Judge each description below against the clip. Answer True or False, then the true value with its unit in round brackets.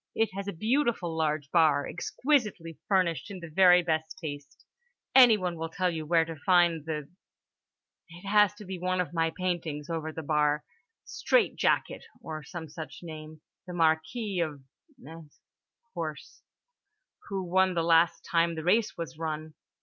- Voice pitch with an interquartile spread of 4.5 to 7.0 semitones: False (2.8 semitones)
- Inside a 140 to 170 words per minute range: True (150 wpm)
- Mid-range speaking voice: True (165 Hz)